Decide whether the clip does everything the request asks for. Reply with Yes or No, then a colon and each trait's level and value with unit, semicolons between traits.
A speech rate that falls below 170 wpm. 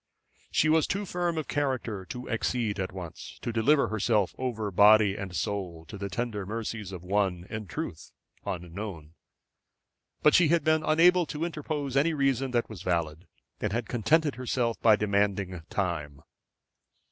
Yes: average, 160 wpm